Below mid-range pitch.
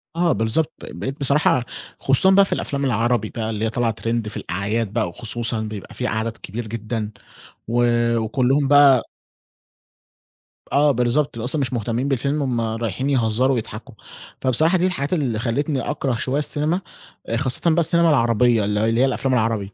Yes: low, 120 Hz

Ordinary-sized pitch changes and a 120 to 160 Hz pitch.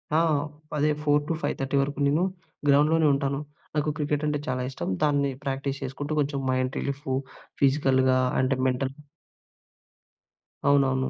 No: narrow, 1.6 semitones; medium, 140 Hz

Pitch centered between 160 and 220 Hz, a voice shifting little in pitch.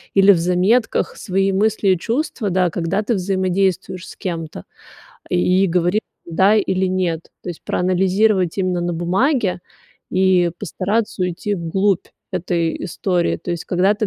Yes: medium, 185 Hz; narrow, 2.1 semitones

